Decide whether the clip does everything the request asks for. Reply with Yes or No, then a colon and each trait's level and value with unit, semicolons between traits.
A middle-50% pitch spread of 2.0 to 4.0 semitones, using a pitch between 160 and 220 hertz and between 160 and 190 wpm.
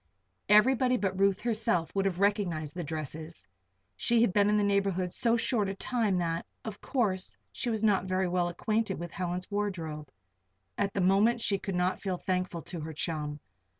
Yes: average, 3.2 semitones; high, 190 Hz; average, 185 wpm